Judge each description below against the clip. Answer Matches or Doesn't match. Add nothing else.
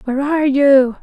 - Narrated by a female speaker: Matches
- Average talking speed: Matches